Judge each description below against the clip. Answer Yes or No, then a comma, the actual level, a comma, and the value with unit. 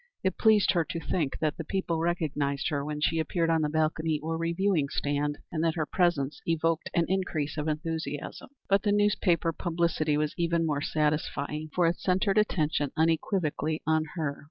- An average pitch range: No, narrow, 2.3 semitones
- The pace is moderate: Yes, average, 180 wpm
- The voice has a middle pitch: Yes, medium, 160 Hz